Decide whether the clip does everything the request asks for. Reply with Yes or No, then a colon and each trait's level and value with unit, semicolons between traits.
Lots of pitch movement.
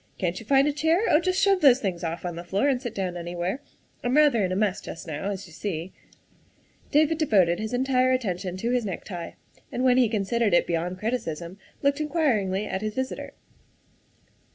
Yes: wide, 6.5 semitones